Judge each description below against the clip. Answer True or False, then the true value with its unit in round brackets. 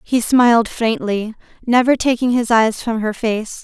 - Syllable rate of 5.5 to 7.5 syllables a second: False (4.4 syllables/s)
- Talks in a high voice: True (235 Hz)